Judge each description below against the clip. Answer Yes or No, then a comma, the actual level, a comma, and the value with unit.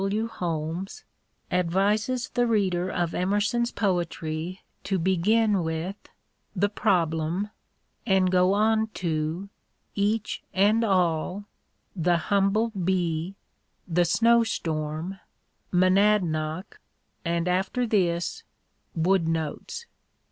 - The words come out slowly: Yes, slow, 110 wpm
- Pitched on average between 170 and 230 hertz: Yes, medium, 185 Hz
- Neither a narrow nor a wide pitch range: Yes, average, 3.6 semitones